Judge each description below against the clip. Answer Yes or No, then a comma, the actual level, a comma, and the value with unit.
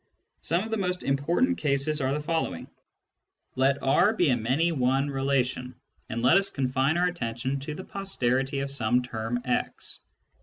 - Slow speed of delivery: No, average, 165 wpm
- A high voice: No, medium, 140 Hz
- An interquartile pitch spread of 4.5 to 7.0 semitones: Yes, average, 4.8 semitones